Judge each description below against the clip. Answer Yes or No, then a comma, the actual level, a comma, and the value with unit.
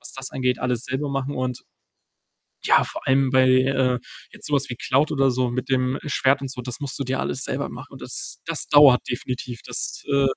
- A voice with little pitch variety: Yes, narrow, 1.4 semitones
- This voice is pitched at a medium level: No, low, 130 Hz